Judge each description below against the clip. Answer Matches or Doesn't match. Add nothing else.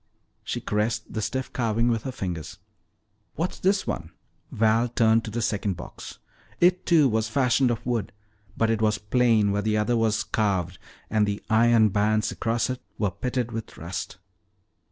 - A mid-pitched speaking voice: Doesn't match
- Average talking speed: Matches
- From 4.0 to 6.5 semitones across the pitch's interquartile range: Doesn't match